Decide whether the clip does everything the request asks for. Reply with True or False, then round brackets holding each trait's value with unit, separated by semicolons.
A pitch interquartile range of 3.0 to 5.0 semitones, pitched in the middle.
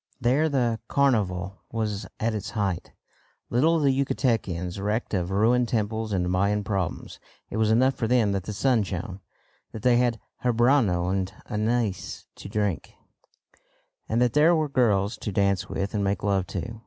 False (3.8 semitones; 110 Hz)